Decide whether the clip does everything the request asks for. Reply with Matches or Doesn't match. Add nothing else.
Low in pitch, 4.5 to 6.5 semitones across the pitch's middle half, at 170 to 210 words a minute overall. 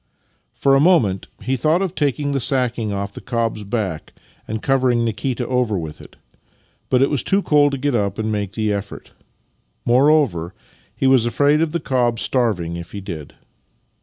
Matches